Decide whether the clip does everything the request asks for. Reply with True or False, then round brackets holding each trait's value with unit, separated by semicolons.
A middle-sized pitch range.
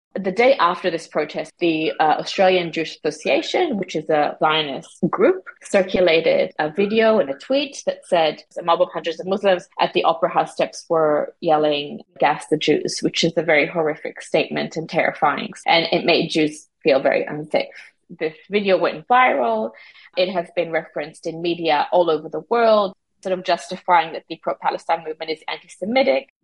True (3.3 semitones)